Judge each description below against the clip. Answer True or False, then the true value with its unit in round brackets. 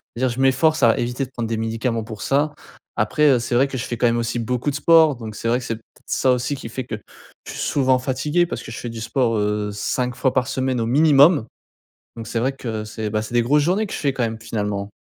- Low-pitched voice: True (125 Hz)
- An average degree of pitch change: True (3.1 semitones)